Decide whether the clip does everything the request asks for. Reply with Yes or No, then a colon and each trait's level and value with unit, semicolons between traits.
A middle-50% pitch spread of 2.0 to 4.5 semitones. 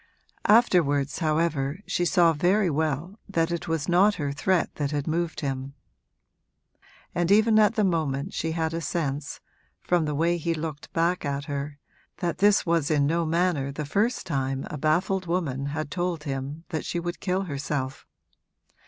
Yes: average, 3.6 semitones